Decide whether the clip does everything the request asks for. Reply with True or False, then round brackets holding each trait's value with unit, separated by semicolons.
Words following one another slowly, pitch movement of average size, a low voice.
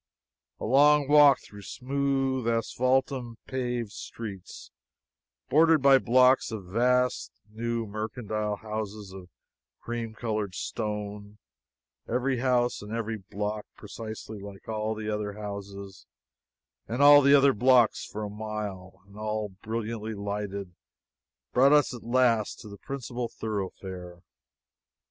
True (120 wpm; 3.5 semitones; 110 Hz)